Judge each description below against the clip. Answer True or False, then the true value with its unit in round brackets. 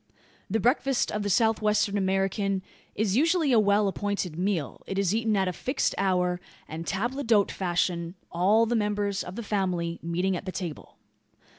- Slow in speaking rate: False (175 wpm)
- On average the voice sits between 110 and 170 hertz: False (200 Hz)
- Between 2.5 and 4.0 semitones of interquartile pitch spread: True (3.1 semitones)